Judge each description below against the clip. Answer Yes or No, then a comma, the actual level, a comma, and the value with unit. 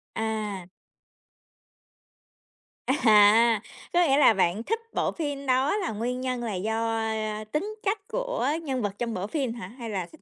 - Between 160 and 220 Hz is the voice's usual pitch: No, high, 230 Hz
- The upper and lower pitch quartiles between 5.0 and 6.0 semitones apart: No, average, 4.4 semitones